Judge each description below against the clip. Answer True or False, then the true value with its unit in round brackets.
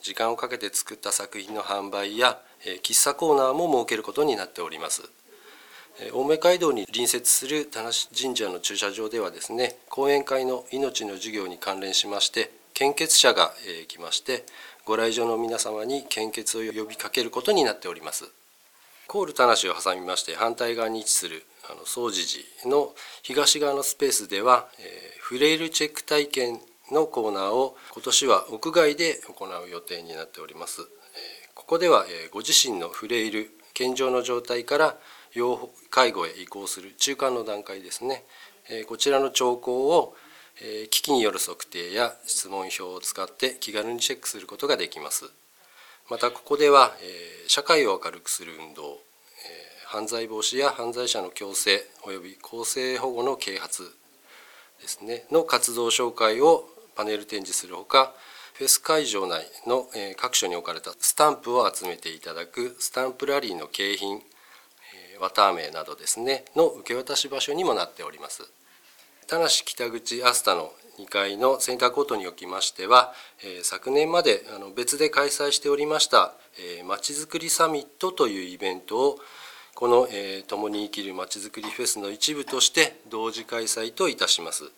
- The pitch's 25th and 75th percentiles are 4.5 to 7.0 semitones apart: True (6.2 semitones)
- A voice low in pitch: True (125 Hz)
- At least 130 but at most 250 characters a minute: False (320 characters per minute)